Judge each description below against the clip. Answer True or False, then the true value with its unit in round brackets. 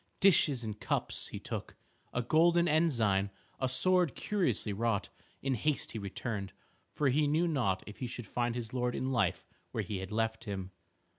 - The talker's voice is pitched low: True (120 Hz)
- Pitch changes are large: True (5.9 semitones)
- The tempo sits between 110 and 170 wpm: False (180 wpm)